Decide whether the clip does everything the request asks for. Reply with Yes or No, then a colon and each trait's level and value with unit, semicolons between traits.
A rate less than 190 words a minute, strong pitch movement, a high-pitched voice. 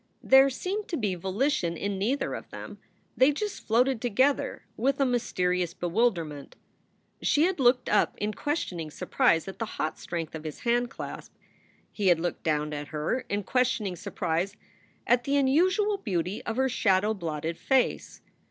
Yes: average, 160 wpm; wide, 7.4 semitones; high, 215 Hz